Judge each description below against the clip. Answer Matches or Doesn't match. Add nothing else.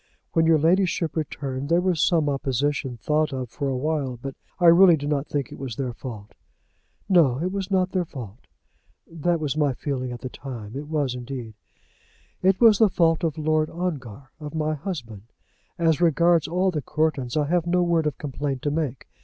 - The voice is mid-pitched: Matches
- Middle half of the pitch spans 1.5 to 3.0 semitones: Doesn't match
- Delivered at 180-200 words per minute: Matches